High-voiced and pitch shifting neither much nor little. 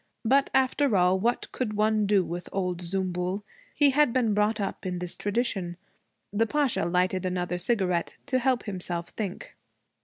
Yes: high, 200 Hz; average, 4.7 semitones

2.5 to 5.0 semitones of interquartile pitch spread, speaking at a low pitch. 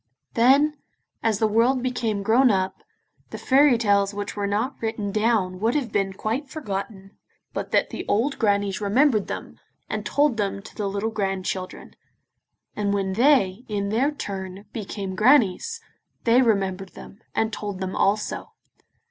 No: average, 3.5 semitones; high, 210 Hz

